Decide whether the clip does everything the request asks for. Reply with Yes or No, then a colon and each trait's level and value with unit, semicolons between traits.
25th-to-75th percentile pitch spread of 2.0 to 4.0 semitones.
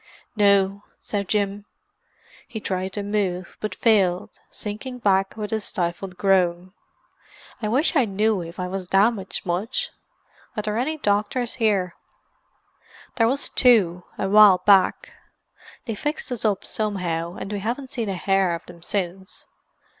Yes: average, 2.8 semitones